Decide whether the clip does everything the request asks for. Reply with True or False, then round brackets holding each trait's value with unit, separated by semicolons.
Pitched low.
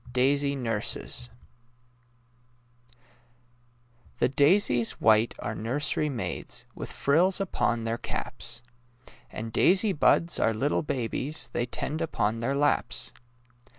True (130 Hz)